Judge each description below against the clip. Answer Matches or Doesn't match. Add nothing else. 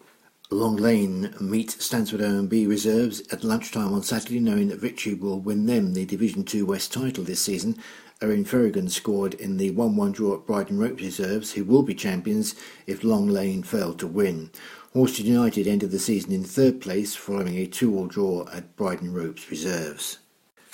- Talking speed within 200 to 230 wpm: Doesn't match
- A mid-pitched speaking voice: Doesn't match